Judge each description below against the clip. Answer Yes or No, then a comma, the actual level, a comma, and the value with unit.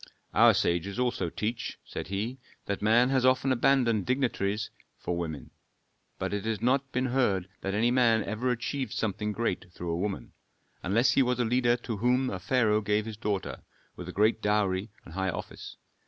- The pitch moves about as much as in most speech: Yes, average, 4.0 semitones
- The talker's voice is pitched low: Yes, low, 110 Hz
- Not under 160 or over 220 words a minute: Yes, average, 185 wpm